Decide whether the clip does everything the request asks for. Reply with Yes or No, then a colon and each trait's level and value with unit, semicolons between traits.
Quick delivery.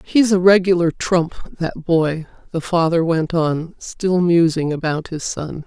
No: average, 160 wpm